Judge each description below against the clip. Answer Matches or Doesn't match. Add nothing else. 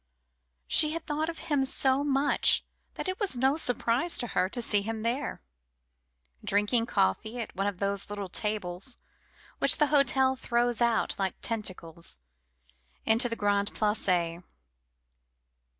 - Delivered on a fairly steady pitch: Doesn't match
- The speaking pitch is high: Matches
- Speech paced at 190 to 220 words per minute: Doesn't match